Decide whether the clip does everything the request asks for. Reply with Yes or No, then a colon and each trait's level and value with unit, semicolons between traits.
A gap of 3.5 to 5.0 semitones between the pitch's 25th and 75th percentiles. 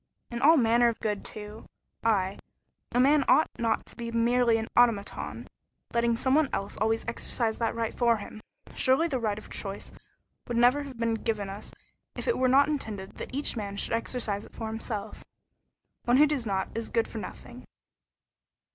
No: narrow, 2.5 semitones